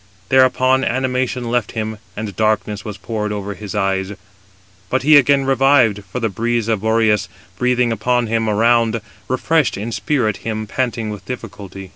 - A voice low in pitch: Yes, low, 115 Hz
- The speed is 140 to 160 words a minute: Yes, average, 155 wpm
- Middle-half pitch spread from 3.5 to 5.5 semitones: No, average, 3.1 semitones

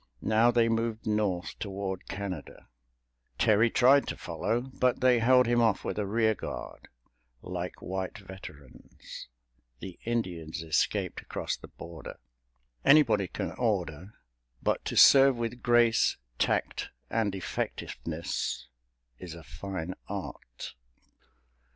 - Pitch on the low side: Yes, low, 105 Hz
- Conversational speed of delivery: No, slow, 120 wpm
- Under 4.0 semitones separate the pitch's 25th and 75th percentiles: No, average, 4.7 semitones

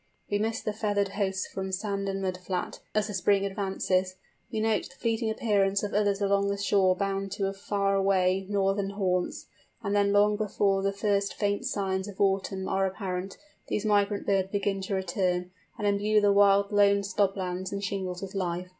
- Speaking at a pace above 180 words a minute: Yes, average, 190 wpm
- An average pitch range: No, narrow, 1.1 semitones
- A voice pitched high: Yes, high, 200 Hz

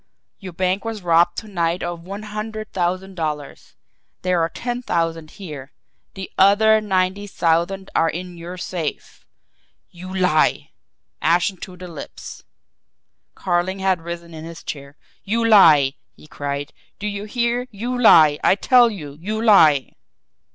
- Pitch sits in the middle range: Yes, medium, 180 Hz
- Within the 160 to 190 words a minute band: No, average, 145 wpm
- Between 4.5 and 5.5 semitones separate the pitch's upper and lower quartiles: No, average, 3.7 semitones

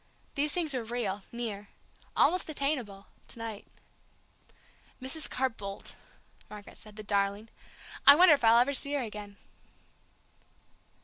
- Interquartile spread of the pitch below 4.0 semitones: No, wide, 5.4 semitones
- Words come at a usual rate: No, slow, 130 wpm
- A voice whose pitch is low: No, high, 230 Hz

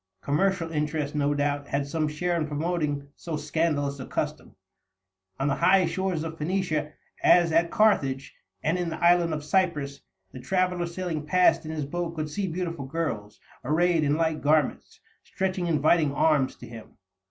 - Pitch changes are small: No, average, 3.1 semitones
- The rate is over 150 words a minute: Yes, average, 165 wpm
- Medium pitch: Yes, medium, 155 Hz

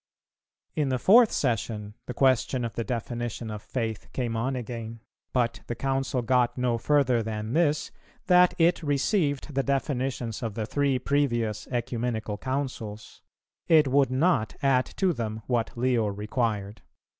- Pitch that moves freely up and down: No, average, 3.3 semitones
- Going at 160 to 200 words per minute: No, average, 145 wpm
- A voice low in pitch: Yes, low, 125 Hz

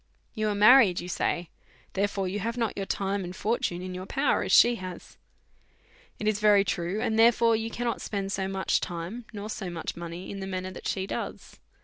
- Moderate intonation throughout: Yes, average, 3.0 semitones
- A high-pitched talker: Yes, high, 195 Hz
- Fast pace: Yes, fast, 210 wpm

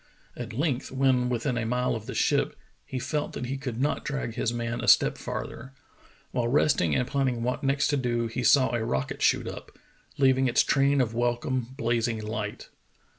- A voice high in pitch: No, low, 125 Hz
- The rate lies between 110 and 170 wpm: No, average, 190 wpm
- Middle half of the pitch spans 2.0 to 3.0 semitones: Yes, narrow, 2.4 semitones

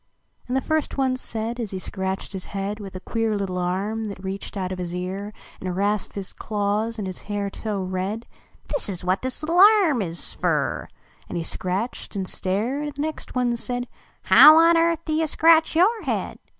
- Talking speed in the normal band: No, fast, 215 wpm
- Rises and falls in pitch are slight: No, wide, 5.4 semitones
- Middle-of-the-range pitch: No, high, 210 Hz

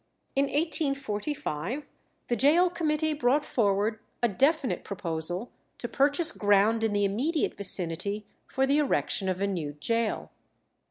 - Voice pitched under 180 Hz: No, high, 230 Hz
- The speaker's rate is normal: No, slow, 130 wpm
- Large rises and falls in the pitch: Yes, wide, 6.5 semitones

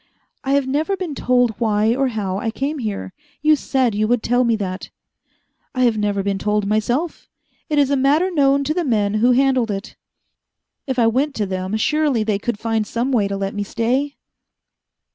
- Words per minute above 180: Yes, average, 200 wpm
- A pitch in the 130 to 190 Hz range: No, high, 240 Hz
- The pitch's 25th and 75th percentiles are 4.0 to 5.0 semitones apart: Yes, average, 4.6 semitones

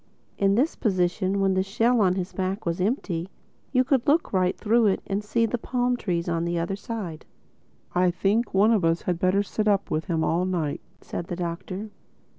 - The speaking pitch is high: Yes, high, 195 Hz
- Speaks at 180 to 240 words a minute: Yes, fast, 205 wpm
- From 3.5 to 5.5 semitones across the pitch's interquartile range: Yes, average, 3.8 semitones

